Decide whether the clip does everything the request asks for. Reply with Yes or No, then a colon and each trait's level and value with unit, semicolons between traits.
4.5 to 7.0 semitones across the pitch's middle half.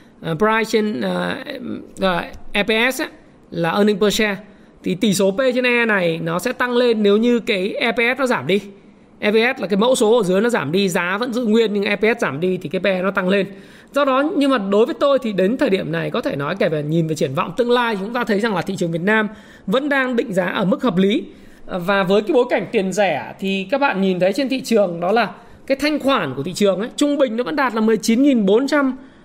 No: average, 4.1 semitones